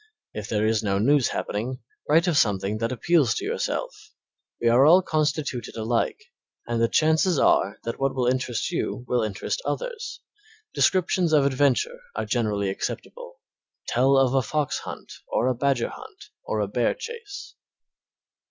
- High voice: No, low, 130 Hz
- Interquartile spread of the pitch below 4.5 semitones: No, wide, 5.5 semitones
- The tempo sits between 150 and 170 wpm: Yes, average, 160 wpm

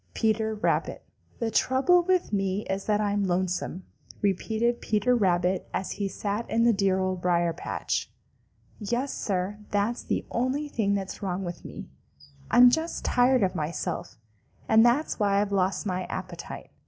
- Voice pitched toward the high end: Yes, high, 205 Hz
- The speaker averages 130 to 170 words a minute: Yes, average, 155 wpm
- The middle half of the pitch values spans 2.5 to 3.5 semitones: No, average, 3.9 semitones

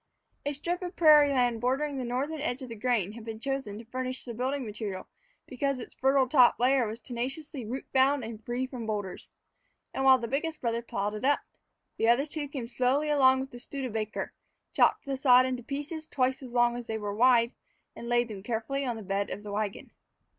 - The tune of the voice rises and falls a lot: No, average, 3.1 semitones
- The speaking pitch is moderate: No, very high, 250 Hz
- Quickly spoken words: Yes, fast, 210 wpm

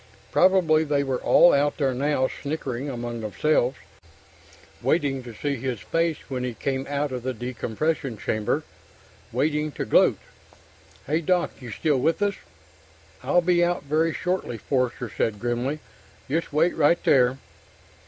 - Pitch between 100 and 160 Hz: Yes, medium, 140 Hz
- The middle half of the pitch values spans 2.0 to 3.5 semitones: No, average, 4.0 semitones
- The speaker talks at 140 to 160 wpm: Yes, average, 145 wpm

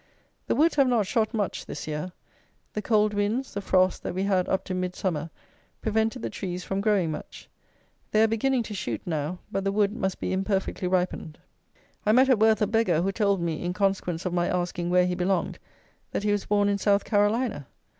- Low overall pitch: No, high, 195 Hz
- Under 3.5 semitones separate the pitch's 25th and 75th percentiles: Yes, average, 2.9 semitones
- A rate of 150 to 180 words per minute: No, fast, 205 wpm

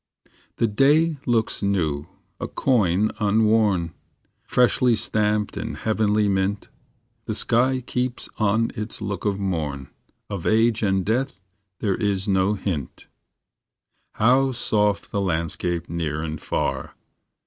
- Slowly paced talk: Yes, slow, 120 wpm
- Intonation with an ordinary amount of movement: Yes, average, 3.1 semitones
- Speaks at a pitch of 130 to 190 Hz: No, low, 105 Hz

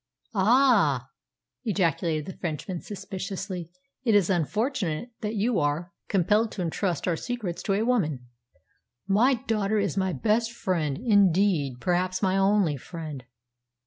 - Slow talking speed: Yes, slow, 130 wpm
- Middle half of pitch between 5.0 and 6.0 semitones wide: No, average, 4.3 semitones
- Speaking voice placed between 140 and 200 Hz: Yes, high, 190 Hz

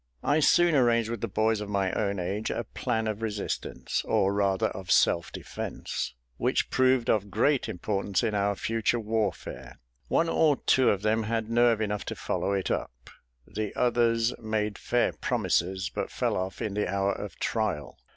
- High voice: No, low, 105 Hz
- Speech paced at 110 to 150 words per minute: No, average, 175 wpm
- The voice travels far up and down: No, average, 2.8 semitones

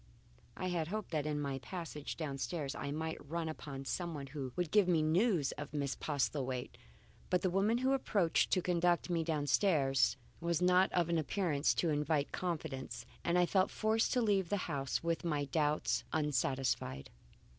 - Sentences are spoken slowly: No, average, 170 wpm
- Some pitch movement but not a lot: Yes, average, 4.0 semitones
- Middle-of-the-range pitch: Yes, medium, 160 Hz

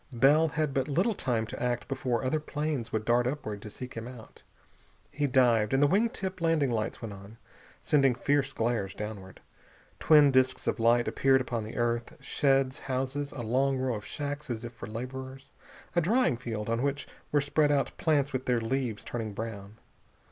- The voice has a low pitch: Yes, low, 130 Hz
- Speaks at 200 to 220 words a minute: No, average, 190 wpm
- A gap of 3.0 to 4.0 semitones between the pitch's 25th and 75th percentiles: Yes, average, 3.6 semitones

